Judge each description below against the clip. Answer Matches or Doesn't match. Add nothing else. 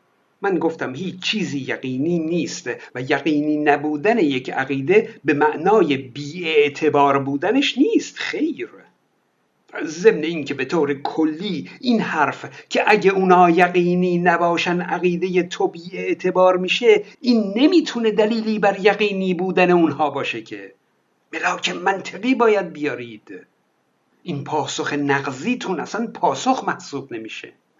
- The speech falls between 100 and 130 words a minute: Matches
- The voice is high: Doesn't match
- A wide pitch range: Matches